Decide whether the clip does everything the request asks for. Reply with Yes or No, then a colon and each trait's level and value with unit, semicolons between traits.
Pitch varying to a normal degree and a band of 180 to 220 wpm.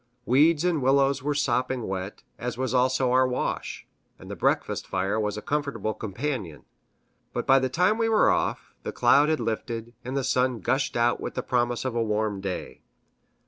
Yes: average, 3.7 semitones; average, 185 wpm